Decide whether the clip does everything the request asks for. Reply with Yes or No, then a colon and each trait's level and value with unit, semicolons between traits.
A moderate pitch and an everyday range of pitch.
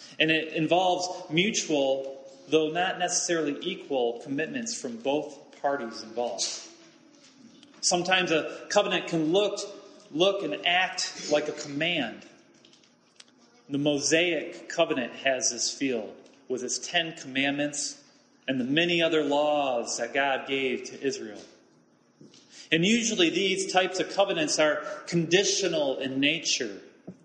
Yes: medium, 165 Hz; average, 4.8 semitones